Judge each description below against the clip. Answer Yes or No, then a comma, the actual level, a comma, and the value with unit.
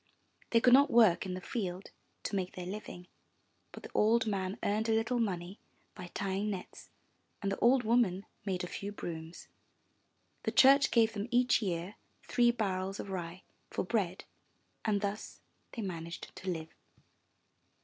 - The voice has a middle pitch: No, high, 200 Hz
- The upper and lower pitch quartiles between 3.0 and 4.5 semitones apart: Yes, average, 3.7 semitones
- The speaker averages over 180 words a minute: No, average, 160 wpm